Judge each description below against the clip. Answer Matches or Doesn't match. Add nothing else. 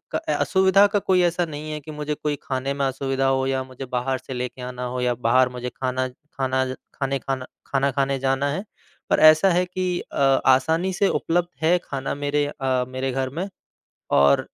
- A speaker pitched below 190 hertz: Matches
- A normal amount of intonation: Matches